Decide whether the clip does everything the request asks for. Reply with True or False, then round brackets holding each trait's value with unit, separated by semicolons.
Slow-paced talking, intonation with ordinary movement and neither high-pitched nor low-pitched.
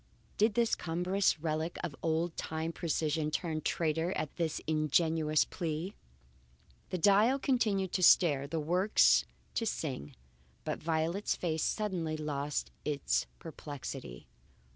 True (120 wpm; 3.0 semitones; 160 Hz)